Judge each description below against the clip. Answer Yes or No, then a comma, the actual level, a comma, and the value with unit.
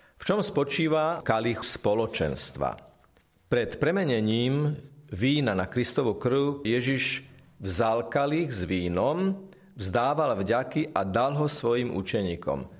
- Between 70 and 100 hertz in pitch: No, low, 135 Hz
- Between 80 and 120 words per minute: Yes, slow, 110 wpm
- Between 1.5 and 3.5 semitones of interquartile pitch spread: No, average, 4.7 semitones